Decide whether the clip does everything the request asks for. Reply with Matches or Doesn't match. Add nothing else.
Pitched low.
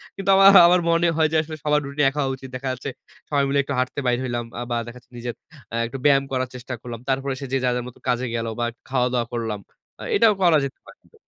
Matches